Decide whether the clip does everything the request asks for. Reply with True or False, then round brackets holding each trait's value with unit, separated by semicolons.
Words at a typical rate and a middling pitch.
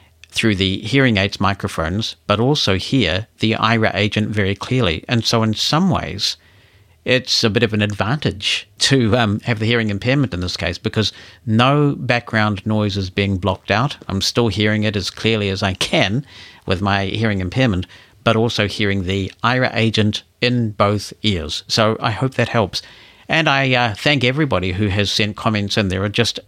False (185 wpm; 105 Hz)